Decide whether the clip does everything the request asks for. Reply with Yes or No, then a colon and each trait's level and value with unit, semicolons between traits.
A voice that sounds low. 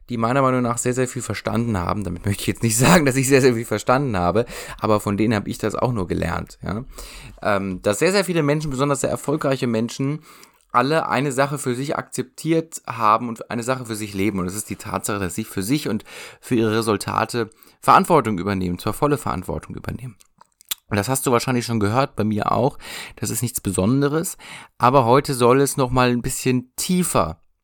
Yes: low, 120 Hz